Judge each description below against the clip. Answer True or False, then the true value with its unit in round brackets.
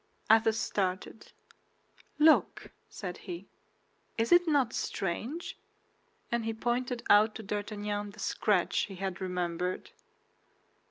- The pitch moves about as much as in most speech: True (3.6 semitones)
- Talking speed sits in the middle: False (110 wpm)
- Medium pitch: False (210 Hz)